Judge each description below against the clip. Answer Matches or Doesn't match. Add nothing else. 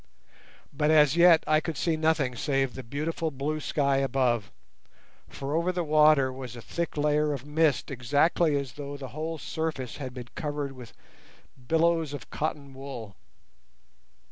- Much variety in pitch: Doesn't match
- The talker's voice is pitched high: Doesn't match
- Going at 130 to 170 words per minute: Matches